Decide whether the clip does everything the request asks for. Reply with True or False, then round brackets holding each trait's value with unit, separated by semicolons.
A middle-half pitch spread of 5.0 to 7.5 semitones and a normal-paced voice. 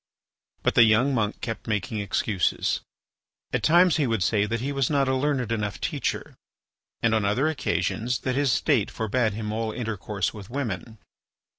False (3.8 semitones; 170 wpm)